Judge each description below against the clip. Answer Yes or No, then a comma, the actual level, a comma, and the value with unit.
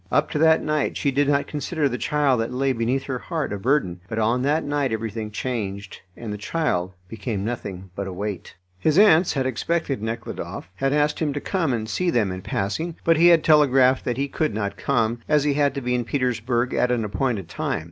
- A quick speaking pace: Yes, fast, 220 wpm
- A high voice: No, low, 125 Hz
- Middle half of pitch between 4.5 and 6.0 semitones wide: Yes, average, 5.0 semitones